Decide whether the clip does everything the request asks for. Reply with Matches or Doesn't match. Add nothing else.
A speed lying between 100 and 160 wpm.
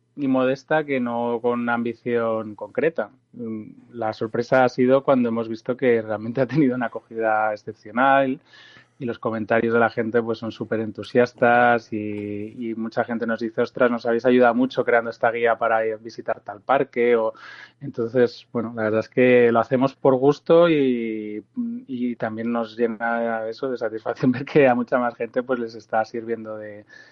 Doesn't match